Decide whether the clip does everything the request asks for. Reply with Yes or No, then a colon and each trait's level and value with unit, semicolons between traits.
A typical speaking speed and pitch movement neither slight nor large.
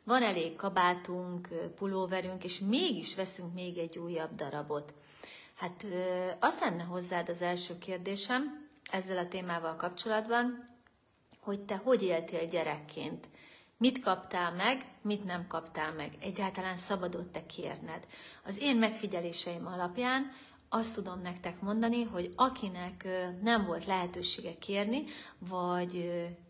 Yes: average, 120 wpm; average, 3.0 semitones